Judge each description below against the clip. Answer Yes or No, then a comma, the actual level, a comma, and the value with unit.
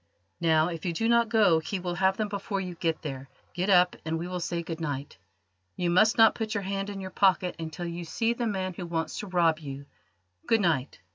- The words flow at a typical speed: No, fast, 230 wpm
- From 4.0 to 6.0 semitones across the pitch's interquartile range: No, average, 3.3 semitones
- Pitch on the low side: No, medium, 180 Hz